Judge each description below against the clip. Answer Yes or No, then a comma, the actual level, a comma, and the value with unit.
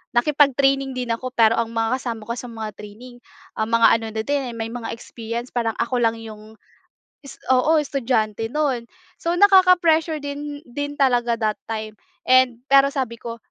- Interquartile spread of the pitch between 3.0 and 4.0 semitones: Yes, average, 3.5 semitones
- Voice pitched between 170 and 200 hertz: No, high, 240 Hz